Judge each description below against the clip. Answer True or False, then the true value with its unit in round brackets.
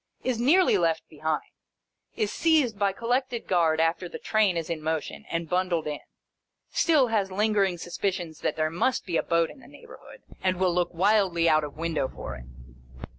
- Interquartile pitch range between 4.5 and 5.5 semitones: True (4.8 semitones)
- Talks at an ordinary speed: True (180 wpm)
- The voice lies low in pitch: False (180 Hz)